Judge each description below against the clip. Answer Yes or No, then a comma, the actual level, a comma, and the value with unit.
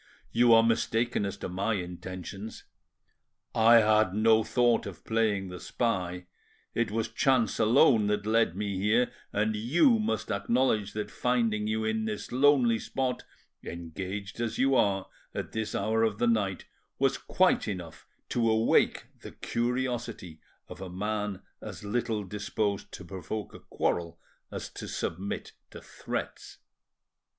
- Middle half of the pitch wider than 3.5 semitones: No, average, 2.7 semitones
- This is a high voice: No, low, 110 Hz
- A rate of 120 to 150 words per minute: Yes, average, 145 wpm